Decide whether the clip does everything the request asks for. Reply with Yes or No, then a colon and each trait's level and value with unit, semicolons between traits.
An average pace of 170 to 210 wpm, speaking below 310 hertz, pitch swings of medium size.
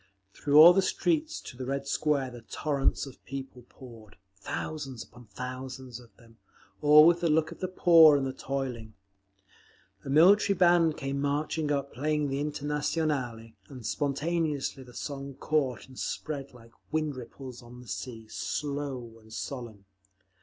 No: average, 155 wpm; medium, 140 Hz; average, 3.5 semitones